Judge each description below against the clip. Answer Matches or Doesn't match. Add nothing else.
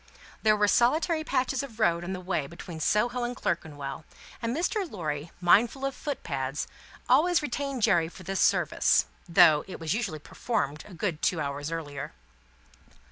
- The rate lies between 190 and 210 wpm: Doesn't match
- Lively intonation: Matches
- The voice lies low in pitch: Doesn't match